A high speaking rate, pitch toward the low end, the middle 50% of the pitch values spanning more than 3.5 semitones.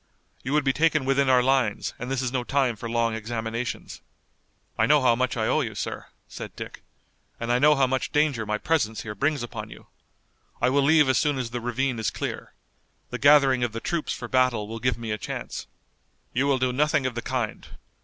No: fast, 220 wpm; low, 125 Hz; average, 2.9 semitones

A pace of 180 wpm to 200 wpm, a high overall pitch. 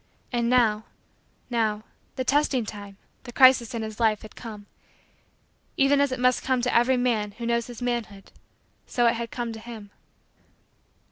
No: average, 165 wpm; high, 235 Hz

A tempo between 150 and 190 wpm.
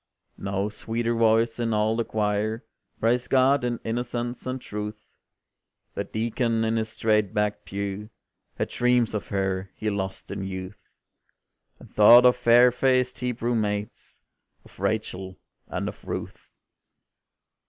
No: slow, 135 wpm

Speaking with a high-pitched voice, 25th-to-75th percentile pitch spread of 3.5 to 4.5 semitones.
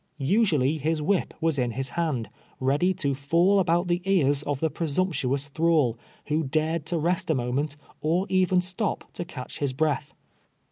No: medium, 155 Hz; average, 3.9 semitones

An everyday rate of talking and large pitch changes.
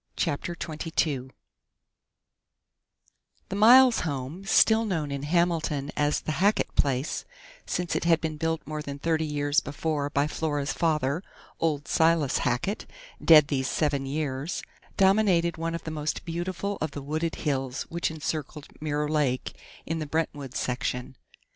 No: average, 145 wpm; average, 2.8 semitones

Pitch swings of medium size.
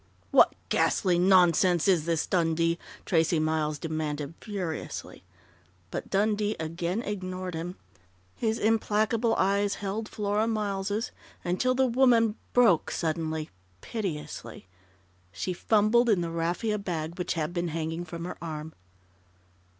Yes: average, 4.4 semitones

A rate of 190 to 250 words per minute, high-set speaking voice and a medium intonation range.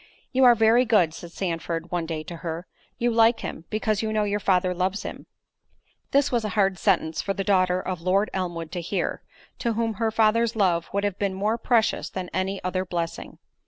Yes: fast, 205 wpm; high, 195 Hz; average, 3.6 semitones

